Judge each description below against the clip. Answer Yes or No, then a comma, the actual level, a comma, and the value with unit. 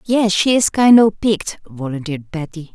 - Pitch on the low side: No, high, 190 Hz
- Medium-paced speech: Yes, average, 175 wpm